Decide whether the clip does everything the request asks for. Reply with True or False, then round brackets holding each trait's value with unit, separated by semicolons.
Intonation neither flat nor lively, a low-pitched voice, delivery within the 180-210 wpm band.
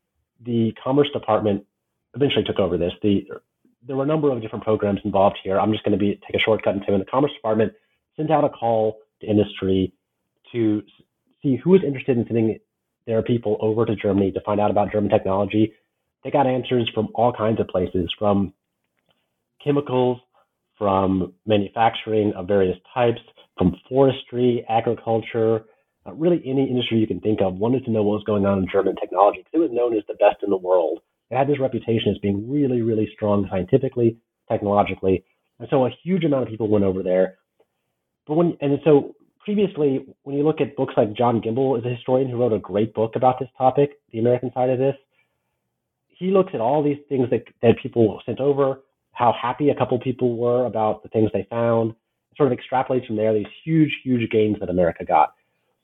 True (4.0 semitones; 115 Hz; 200 wpm)